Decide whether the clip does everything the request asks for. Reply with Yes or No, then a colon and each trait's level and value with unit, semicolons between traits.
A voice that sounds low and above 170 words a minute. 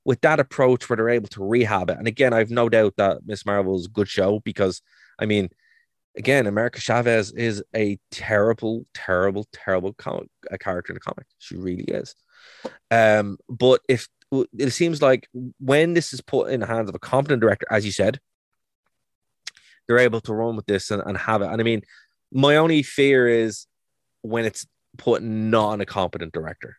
Yes: low, 115 Hz; average, 195 wpm